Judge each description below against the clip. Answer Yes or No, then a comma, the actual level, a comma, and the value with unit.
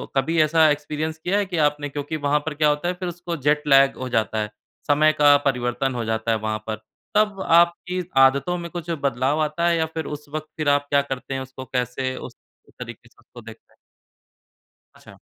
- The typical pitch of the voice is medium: Yes, medium, 145 Hz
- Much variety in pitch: No, average, 3.6 semitones